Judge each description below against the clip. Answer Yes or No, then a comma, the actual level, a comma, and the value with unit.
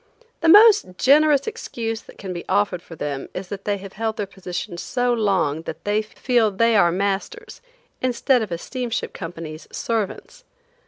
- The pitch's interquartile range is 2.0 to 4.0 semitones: No, average, 5.2 semitones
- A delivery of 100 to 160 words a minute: No, average, 170 wpm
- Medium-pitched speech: No, high, 205 Hz